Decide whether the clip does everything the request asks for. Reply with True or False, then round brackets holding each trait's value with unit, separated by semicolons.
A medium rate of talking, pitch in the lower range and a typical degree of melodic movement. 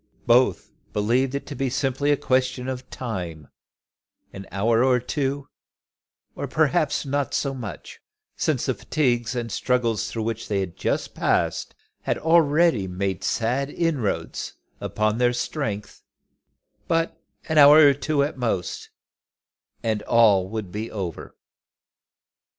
False (130 wpm; 125 Hz; 4.7 semitones)